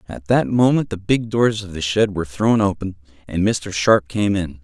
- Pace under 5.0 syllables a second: Yes, 4.8 syllables/s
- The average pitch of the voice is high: No, low, 100 Hz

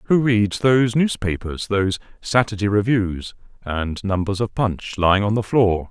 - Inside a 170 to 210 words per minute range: No, average, 150 wpm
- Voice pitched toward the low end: Yes, low, 105 Hz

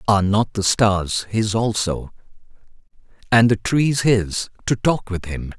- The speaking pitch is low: Yes, low, 105 Hz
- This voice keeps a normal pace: Yes, average, 150 wpm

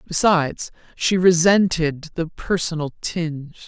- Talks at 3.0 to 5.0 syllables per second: Yes, 4.0 syllables/s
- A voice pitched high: No, medium, 165 Hz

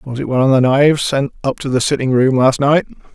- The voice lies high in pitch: No, low, 135 Hz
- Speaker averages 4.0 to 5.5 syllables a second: No, 6.2 syllables/s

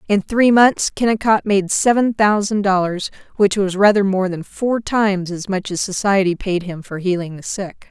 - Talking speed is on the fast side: No, average, 190 wpm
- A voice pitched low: No, high, 200 Hz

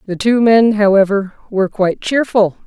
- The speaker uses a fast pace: No, average, 160 wpm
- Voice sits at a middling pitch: No, high, 210 Hz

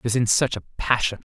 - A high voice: No, low, 110 Hz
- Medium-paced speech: No, fast, 275 wpm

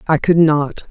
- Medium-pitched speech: Yes, medium, 155 Hz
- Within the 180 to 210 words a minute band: Yes, average, 200 wpm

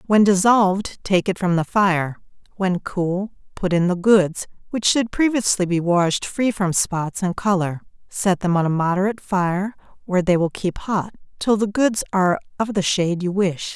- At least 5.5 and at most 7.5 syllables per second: No, 4.6 syllables/s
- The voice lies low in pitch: No, high, 190 Hz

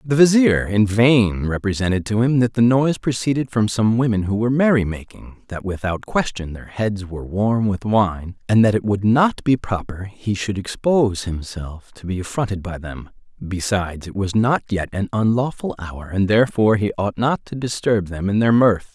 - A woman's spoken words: No, male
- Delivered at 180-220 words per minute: Yes, average, 195 wpm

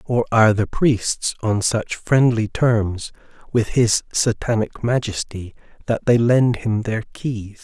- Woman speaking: No, male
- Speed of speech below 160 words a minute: Yes, average, 140 wpm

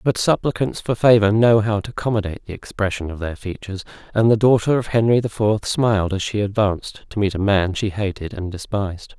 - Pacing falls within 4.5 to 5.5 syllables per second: No, 5.8 syllables/s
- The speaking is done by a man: Yes, male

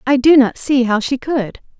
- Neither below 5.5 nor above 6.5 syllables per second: No, 4.6 syllables/s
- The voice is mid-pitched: No, very high, 255 Hz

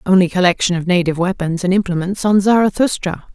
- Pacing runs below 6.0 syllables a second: No, 6.3 syllables/s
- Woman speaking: Yes, female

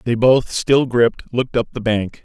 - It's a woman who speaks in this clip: No, male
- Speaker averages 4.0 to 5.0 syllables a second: Yes, 4.9 syllables/s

